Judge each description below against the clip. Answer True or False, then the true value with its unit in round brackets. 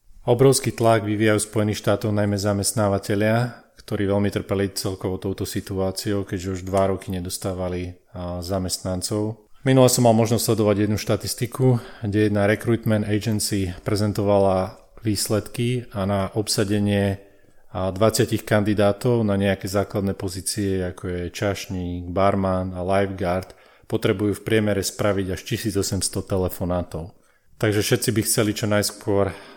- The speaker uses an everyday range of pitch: False (2.1 semitones)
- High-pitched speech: False (100 Hz)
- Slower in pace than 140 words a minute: True (120 wpm)